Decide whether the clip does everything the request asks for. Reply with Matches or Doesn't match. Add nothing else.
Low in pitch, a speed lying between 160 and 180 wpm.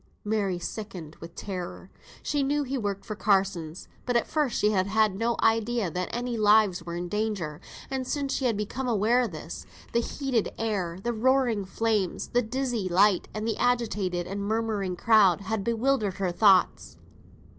Doesn't match